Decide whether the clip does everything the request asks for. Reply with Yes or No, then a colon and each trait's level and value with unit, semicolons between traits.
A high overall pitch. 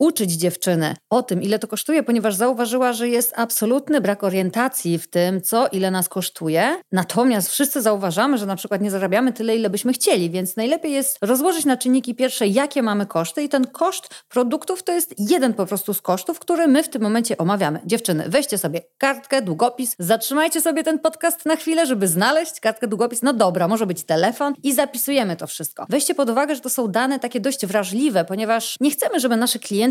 Yes: high, 240 Hz